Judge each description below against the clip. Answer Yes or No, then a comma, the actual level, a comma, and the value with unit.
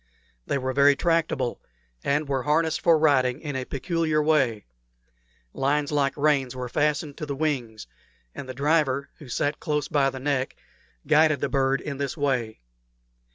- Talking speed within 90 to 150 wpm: No, average, 160 wpm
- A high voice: No, medium, 140 Hz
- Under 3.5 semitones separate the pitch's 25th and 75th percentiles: Yes, narrow, 2.4 semitones